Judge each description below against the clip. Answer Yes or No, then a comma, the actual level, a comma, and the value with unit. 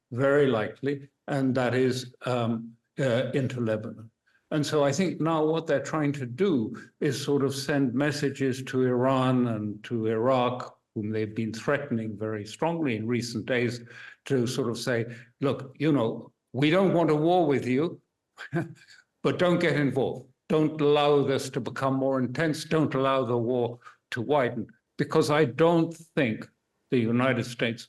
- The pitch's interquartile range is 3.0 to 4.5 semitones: Yes, average, 3.5 semitones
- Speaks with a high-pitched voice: No, low, 135 Hz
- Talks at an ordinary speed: Yes, average, 165 wpm